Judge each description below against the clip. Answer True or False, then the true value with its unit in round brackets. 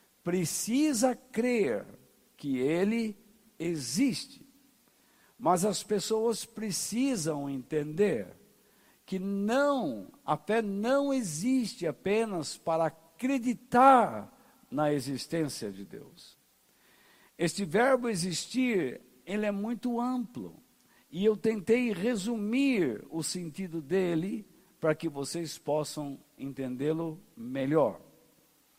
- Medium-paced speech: False (90 wpm)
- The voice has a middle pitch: False (210 Hz)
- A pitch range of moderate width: False (6.9 semitones)